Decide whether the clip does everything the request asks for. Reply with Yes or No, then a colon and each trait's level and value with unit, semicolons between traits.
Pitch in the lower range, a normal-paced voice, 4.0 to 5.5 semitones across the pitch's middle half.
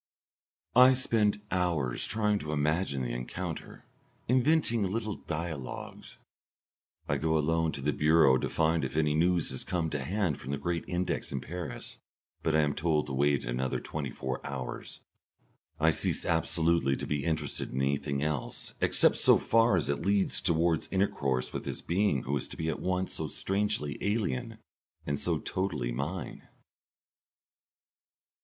Yes: very low, 80 Hz; average, 160 wpm; average, 4.8 semitones